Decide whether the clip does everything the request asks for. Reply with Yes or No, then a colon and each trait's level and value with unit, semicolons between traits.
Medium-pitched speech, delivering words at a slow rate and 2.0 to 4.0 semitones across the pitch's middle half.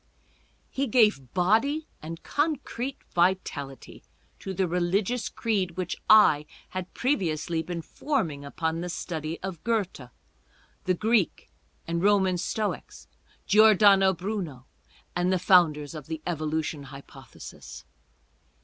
No: medium, 180 Hz; slow, 115 wpm; average, 4.7 semitones